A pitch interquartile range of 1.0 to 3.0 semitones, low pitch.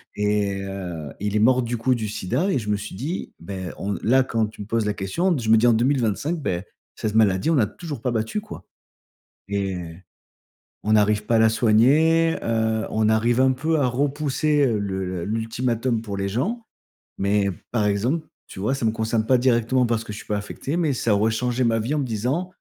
No: average, 4.0 semitones; low, 115 Hz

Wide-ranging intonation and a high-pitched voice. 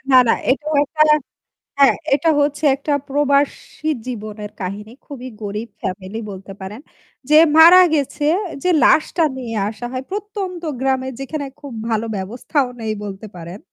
Yes: wide, 5.7 semitones; very high, 260 Hz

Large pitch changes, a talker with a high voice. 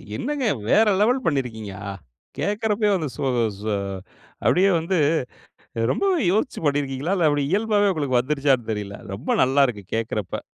No: wide, 8.8 semitones; medium, 145 Hz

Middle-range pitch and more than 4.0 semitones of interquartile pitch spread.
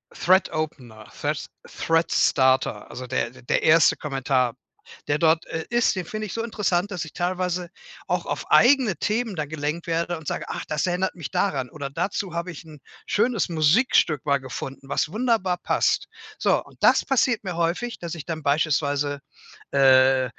Yes: medium, 165 Hz; average, 4.5 semitones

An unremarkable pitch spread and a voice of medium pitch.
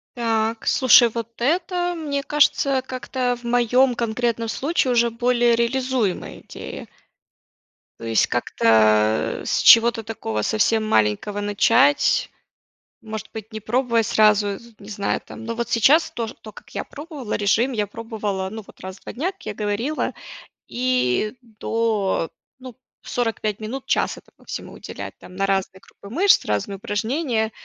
No: average, 3.4 semitones; high, 230 Hz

